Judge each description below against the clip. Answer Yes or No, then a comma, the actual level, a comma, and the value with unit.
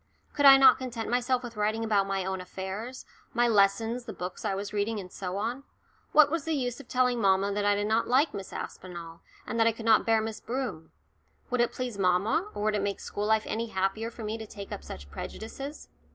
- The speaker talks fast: Yes, fast, 230 wpm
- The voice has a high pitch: Yes, high, 220 Hz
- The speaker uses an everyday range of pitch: Yes, average, 3.7 semitones